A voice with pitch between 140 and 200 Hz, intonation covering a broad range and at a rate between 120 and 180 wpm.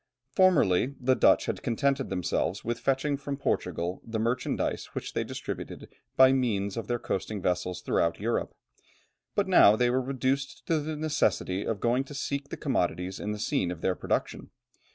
No: low, 120 Hz; wide, 5.9 semitones; average, 175 wpm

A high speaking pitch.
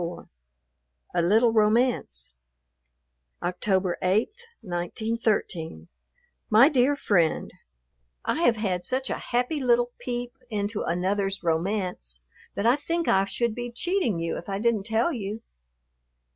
Yes: high, 215 Hz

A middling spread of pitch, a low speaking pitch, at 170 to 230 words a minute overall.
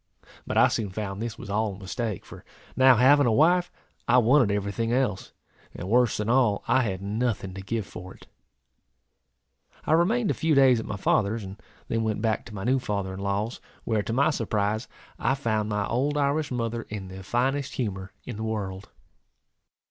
Yes: average, 4.1 semitones; low, 110 Hz; average, 195 wpm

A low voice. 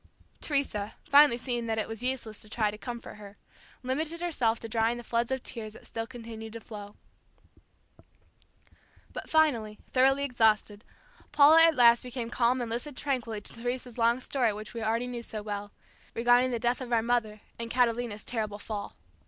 No: high, 235 Hz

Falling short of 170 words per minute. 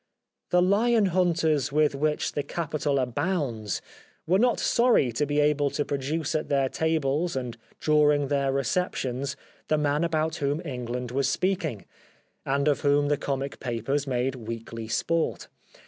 Yes: average, 145 wpm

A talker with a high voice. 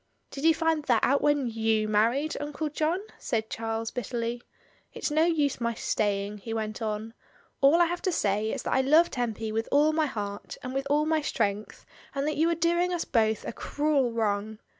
Yes: very high, 250 Hz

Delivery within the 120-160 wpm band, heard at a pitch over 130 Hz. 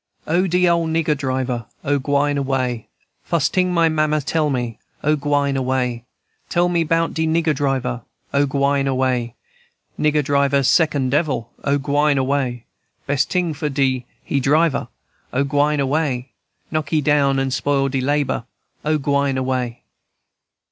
Yes: average, 150 wpm; medium, 140 Hz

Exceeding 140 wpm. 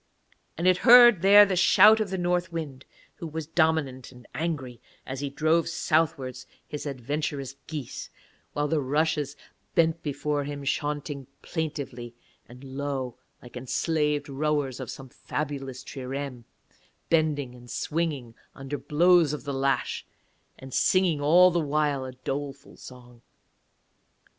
No: slow, 135 wpm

